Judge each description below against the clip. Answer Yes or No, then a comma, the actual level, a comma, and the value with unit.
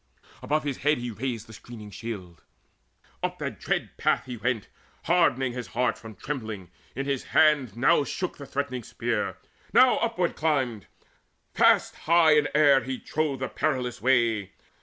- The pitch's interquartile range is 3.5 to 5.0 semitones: Yes, average, 4.4 semitones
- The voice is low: Yes, low, 130 Hz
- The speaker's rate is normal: Yes, average, 160 wpm